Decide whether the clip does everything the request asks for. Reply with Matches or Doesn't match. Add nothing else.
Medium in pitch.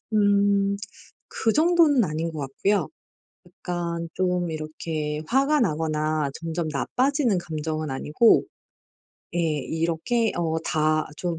Matches